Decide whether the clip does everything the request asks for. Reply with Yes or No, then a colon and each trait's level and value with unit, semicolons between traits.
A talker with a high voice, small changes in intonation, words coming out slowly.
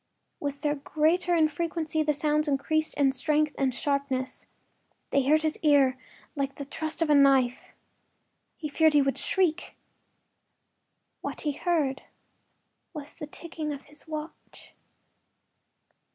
Yes: very high, 300 Hz; narrow, 2.0 semitones; slow, 130 wpm